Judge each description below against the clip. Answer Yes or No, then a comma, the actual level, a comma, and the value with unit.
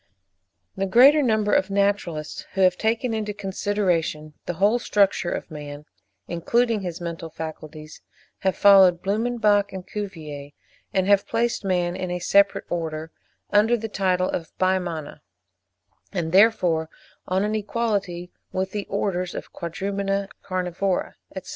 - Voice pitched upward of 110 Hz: Yes, high, 190 Hz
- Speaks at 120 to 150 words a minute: Yes, average, 140 wpm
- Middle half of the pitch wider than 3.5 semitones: No, average, 3.0 semitones